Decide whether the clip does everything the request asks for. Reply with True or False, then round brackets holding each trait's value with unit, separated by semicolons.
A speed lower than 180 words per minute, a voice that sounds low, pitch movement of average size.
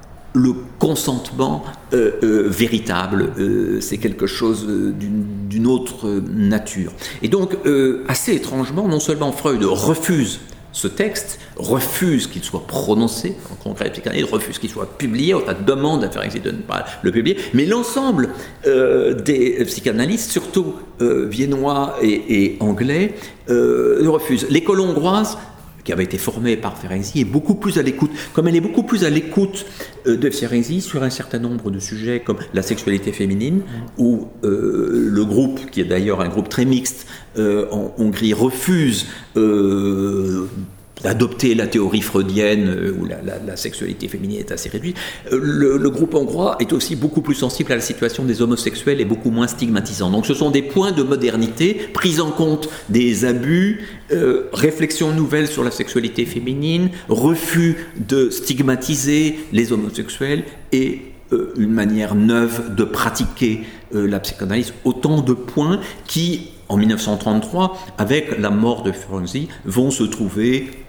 False (160 wpm; 125 Hz; 6.5 semitones)